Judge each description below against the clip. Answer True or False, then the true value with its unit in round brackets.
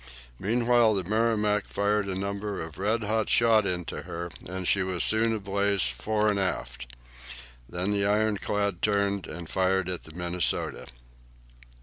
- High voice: False (100 Hz)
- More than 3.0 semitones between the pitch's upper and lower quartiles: False (2.6 semitones)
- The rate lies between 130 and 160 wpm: True (145 wpm)